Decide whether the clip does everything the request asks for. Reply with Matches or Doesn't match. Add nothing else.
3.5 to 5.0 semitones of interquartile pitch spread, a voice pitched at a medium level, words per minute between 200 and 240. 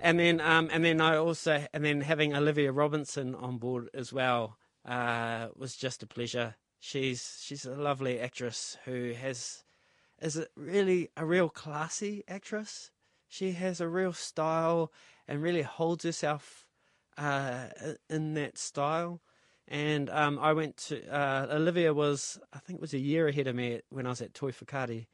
Doesn't match